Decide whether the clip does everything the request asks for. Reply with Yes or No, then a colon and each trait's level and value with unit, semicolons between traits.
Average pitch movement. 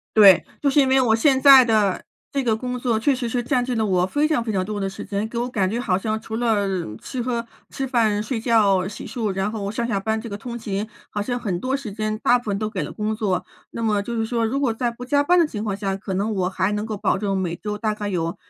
Yes: average, 3.2 semitones